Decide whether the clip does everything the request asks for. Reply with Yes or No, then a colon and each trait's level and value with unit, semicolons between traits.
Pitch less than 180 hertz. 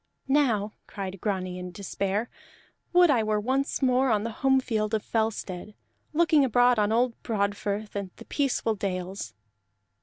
No: high, 215 Hz